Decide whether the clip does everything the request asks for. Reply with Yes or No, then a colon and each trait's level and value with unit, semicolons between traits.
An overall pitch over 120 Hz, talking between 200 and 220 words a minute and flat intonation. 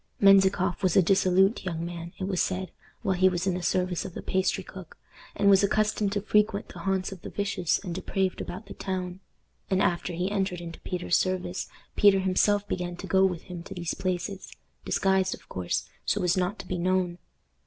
Yes: medium, 185 Hz; fast, 205 wpm; narrow, 1.5 semitones